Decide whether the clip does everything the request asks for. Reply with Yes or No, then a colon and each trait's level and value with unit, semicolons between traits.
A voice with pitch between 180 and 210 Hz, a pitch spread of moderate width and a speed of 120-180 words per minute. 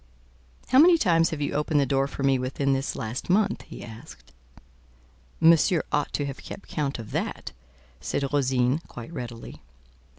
No: medium, 140 Hz; average, 4.1 semitones; average, 165 wpm